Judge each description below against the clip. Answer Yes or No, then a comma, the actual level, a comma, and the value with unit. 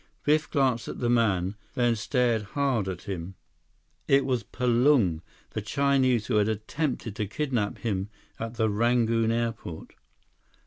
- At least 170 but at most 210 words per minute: No, average, 140 wpm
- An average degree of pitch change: Yes, average, 3.5 semitones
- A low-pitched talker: Yes, low, 115 Hz